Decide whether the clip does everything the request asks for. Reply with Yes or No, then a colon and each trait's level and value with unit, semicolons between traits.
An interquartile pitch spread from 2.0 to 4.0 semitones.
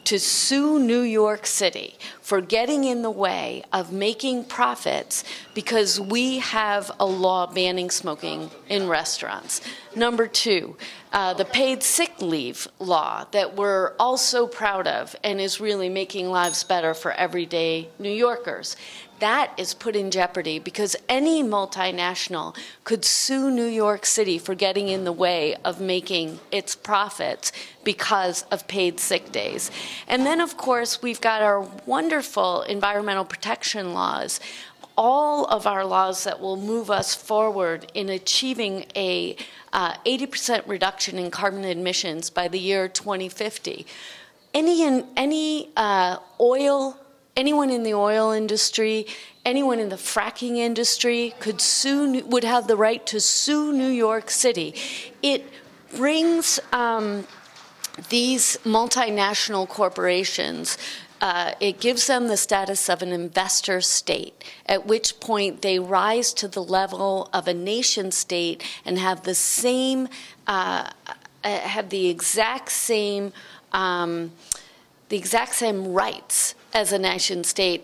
No: average, 4.4 semitones